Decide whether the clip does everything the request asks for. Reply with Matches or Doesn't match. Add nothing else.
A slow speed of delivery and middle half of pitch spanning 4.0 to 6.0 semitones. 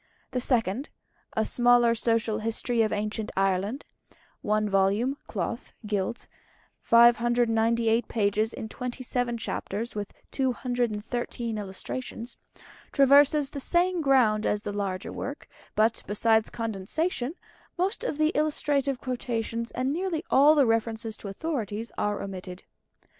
Doesn't match